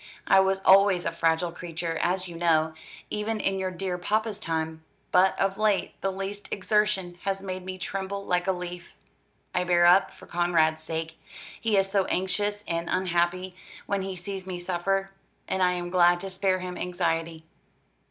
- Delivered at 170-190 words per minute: Yes, average, 175 wpm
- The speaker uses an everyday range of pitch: No, narrow, 1.9 semitones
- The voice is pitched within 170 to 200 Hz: Yes, medium, 185 Hz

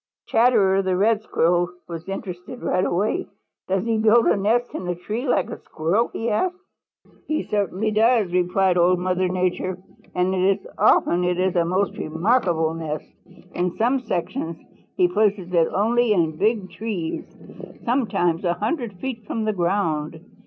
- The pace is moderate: Yes, average, 155 wpm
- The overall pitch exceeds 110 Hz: Yes, high, 190 Hz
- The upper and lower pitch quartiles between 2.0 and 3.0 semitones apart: No, average, 3.9 semitones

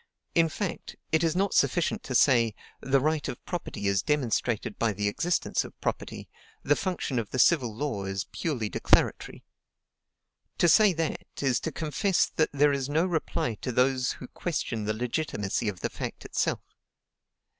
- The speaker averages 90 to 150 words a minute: No, average, 165 wpm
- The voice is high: No, low, 135 Hz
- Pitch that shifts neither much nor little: No, wide, 5.8 semitones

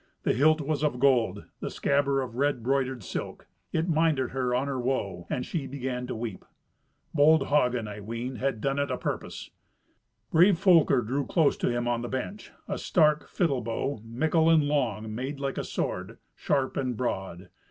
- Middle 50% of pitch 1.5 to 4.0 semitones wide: Yes, average, 3.5 semitones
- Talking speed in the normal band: Yes, average, 180 wpm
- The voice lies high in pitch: No, low, 135 Hz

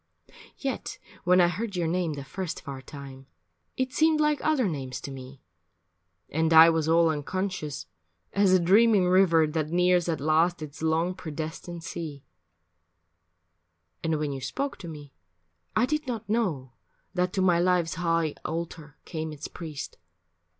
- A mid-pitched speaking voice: Yes, medium, 165 Hz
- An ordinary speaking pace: Yes, average, 155 wpm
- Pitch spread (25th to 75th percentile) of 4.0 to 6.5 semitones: No, average, 3.3 semitones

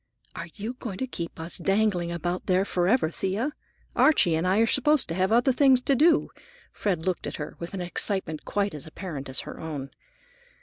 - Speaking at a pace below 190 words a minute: No, average, 200 wpm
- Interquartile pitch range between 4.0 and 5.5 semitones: Yes, average, 5.1 semitones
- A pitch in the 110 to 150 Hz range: No, medium, 185 Hz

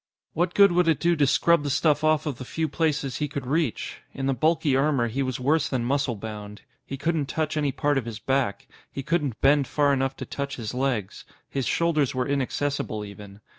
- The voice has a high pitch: No, medium, 140 Hz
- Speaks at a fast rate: Yes, fast, 215 wpm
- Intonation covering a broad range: No, average, 3.3 semitones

